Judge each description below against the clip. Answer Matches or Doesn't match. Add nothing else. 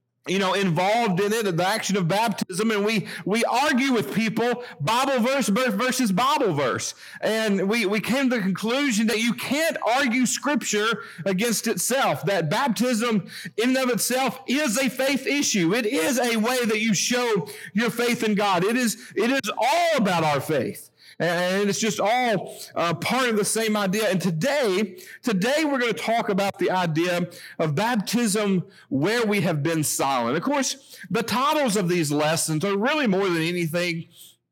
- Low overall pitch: Doesn't match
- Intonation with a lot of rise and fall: Doesn't match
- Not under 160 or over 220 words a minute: Matches